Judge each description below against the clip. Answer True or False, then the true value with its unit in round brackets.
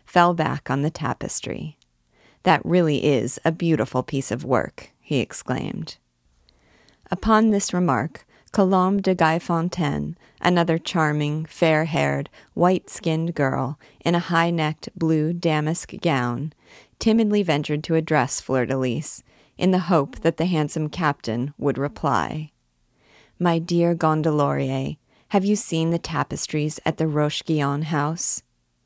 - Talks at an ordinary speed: False (120 wpm)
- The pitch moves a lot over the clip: False (3.8 semitones)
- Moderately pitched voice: True (155 Hz)